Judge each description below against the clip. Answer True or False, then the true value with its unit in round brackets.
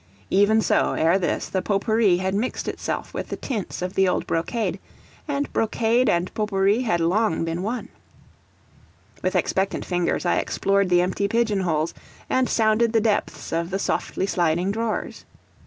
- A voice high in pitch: True (200 Hz)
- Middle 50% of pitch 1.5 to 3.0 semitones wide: False (3.8 semitones)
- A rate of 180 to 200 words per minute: False (170 wpm)